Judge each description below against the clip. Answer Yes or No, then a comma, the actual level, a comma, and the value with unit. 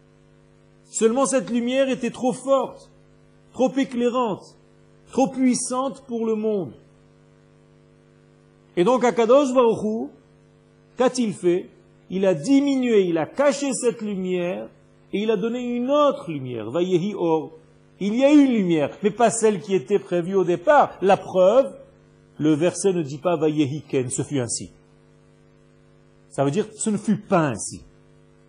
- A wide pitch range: Yes, wide, 6.3 semitones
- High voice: Yes, high, 210 Hz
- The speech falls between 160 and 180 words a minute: No, slow, 145 wpm